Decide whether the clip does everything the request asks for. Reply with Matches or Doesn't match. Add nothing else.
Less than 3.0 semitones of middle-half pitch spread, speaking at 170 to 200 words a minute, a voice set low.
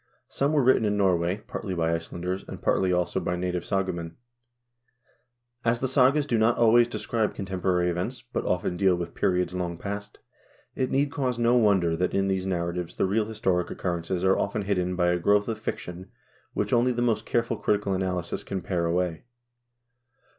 Doesn't match